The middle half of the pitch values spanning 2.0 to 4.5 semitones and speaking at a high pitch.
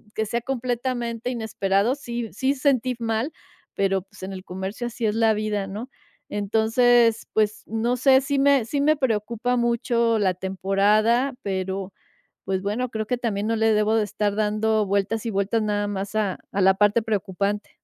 Yes: average, 2.9 semitones; high, 220 Hz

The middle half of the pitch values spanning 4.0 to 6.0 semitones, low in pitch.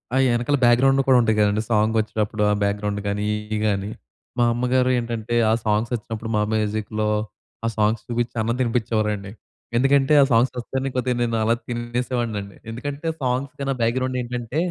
No: average, 2.8 semitones; low, 115 Hz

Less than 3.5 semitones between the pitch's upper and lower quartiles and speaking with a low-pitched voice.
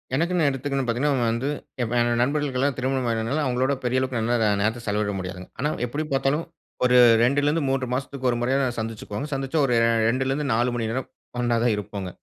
Yes: average, 2.9 semitones; low, 130 Hz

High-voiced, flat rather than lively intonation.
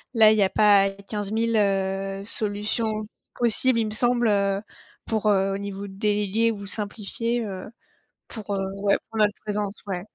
Yes: high, 205 Hz; narrow, 1.8 semitones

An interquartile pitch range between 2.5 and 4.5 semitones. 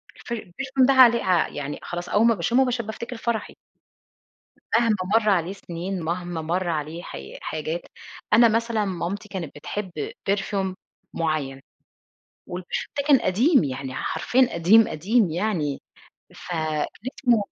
No: wide, 5.6 semitones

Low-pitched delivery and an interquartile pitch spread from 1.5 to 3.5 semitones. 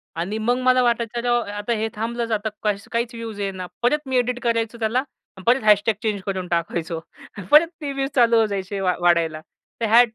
No: high, 225 Hz; average, 3.2 semitones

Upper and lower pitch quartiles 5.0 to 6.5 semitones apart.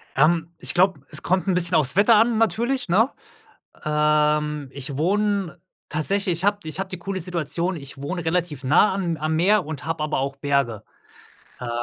No: average, 4.1 semitones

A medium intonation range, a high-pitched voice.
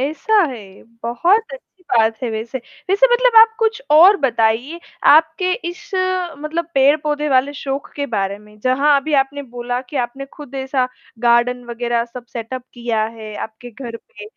Yes: average, 4.6 semitones; very high, 260 Hz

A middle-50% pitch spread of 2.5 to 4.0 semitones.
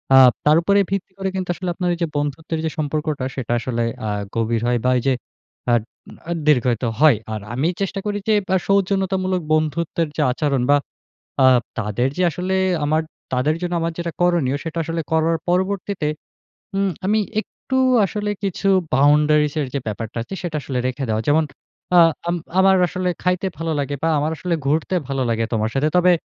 No: average, 5.1 semitones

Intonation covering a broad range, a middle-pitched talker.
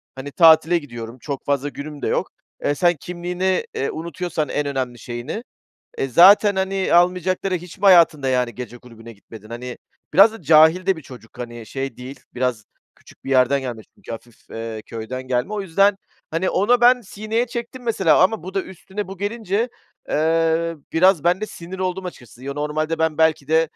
Yes: wide, 6.6 semitones; medium, 160 Hz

